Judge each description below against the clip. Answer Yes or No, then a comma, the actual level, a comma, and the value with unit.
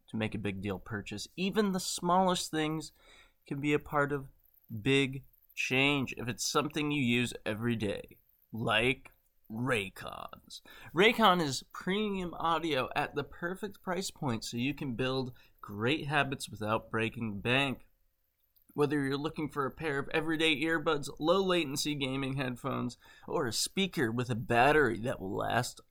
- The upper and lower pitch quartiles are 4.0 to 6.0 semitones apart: Yes, wide, 5.6 semitones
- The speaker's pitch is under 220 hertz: Yes, medium, 140 Hz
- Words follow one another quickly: No, average, 155 wpm